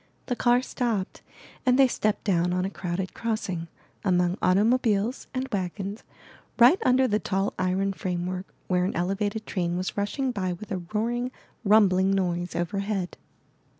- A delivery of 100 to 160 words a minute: Yes, average, 150 wpm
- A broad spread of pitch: No, average, 3.6 semitones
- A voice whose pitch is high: Yes, high, 195 Hz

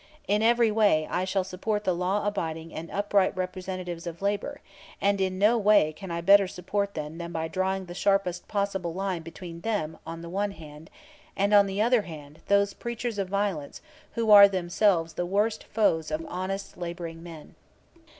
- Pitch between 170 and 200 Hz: Yes, high, 190 Hz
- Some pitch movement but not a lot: Yes, average, 3.2 semitones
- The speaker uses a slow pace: No, average, 185 wpm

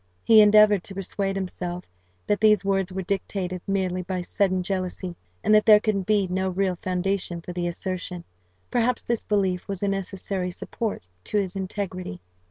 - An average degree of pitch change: No, narrow, 2.0 semitones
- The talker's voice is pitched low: No, high, 190 Hz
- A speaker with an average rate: Yes, average, 170 wpm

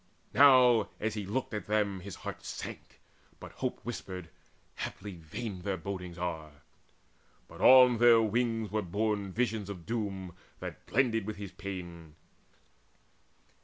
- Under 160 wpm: Yes, slow, 135 wpm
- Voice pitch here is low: Yes, low, 100 Hz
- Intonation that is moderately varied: Yes, average, 3.5 semitones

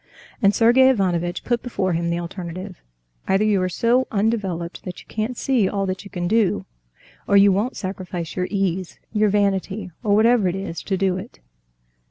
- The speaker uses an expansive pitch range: No, average, 2.9 semitones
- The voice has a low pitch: No, high, 195 Hz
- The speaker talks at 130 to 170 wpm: No, average, 185 wpm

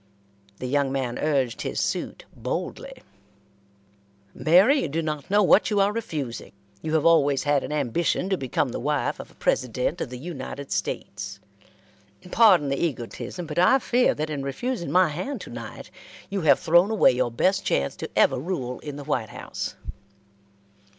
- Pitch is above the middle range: No, medium, 150 Hz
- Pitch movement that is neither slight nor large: No, wide, 5.7 semitones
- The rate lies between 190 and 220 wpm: No, average, 170 wpm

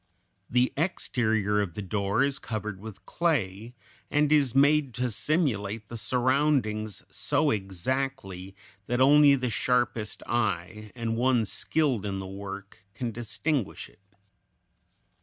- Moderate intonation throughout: Yes, average, 4.9 semitones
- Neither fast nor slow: No, slow, 125 wpm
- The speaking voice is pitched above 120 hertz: No, low, 115 Hz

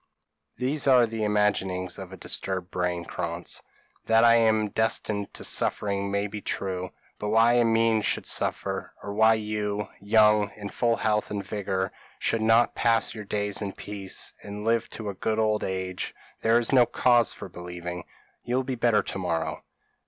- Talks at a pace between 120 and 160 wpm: No, average, 175 wpm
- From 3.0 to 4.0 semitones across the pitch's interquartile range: No, narrow, 2.5 semitones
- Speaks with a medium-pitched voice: No, low, 105 Hz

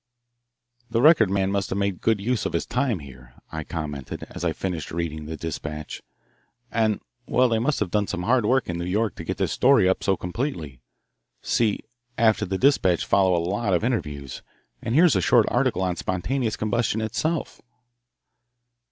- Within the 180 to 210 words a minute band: Yes, average, 185 wpm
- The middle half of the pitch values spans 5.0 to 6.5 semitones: Yes, average, 5.3 semitones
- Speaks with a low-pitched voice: Yes, low, 100 Hz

